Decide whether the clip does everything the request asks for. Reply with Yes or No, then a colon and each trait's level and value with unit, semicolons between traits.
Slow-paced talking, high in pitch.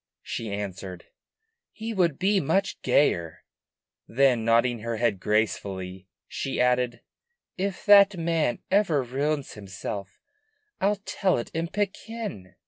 No: slow, 120 wpm; low, 125 Hz